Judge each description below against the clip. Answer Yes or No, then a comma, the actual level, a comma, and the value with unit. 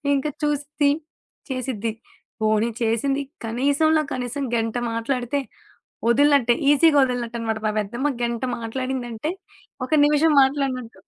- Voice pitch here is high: Yes, very high, 255 Hz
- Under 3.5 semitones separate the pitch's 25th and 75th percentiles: No, average, 3.8 semitones